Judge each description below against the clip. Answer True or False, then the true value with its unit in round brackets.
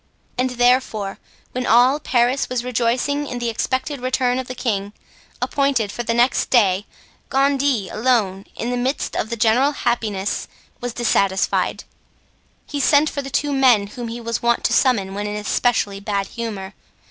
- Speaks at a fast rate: False (165 wpm)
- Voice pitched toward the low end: False (240 Hz)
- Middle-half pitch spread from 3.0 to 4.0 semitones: True (3.5 semitones)